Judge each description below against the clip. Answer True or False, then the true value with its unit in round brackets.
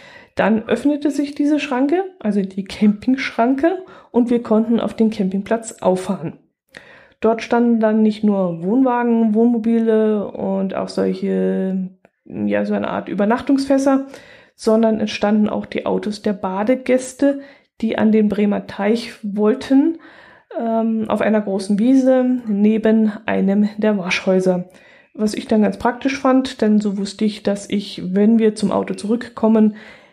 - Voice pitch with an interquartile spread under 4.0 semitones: True (3.5 semitones)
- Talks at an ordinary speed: True (140 wpm)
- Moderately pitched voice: False (220 Hz)